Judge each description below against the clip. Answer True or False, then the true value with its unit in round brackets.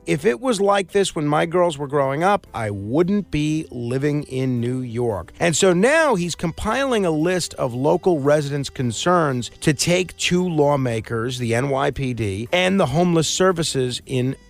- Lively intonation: True (5.7 semitones)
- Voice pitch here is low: False (150 Hz)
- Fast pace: False (165 wpm)